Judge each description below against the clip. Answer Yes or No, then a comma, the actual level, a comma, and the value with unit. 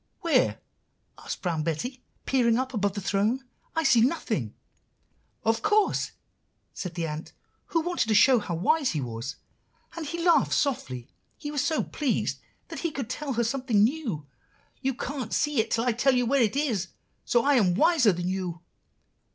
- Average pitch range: No, wide, 6.8 semitones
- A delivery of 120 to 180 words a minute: Yes, average, 175 wpm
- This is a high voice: Yes, high, 240 Hz